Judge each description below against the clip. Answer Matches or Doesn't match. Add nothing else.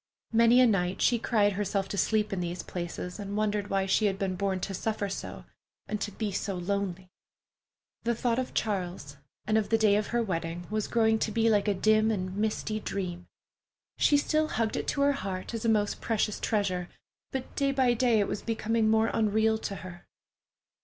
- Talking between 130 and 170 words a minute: Doesn't match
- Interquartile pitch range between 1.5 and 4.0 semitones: Matches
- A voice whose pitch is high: Matches